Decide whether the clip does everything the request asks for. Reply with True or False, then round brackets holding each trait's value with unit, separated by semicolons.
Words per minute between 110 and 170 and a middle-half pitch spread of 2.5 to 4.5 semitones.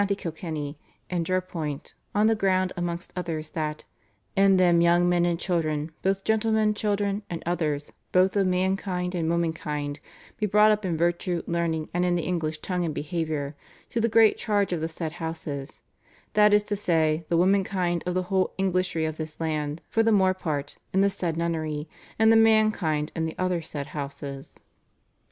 False (185 wpm; 3.4 semitones)